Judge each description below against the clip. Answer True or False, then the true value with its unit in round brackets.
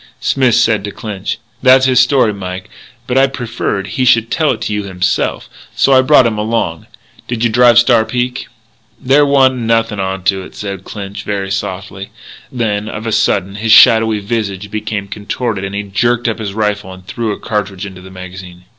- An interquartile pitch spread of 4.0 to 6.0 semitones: False (3.6 semitones)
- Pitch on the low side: True (105 Hz)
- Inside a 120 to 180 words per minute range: False (190 wpm)